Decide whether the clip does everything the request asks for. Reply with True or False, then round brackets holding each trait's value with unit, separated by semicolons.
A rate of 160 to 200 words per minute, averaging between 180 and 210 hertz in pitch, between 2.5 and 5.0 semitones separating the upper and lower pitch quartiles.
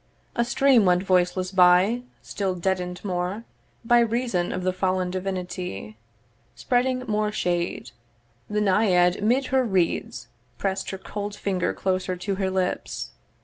False (135 wpm; 190 Hz; 2.8 semitones)